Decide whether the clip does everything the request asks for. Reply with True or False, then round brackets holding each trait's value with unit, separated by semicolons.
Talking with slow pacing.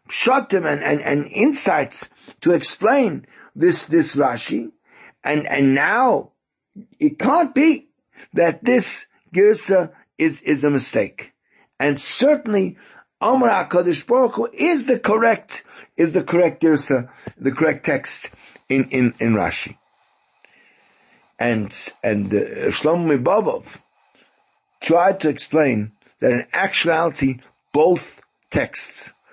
True (110 wpm)